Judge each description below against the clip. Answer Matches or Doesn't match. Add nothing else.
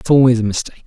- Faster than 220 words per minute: Matches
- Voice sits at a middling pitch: Doesn't match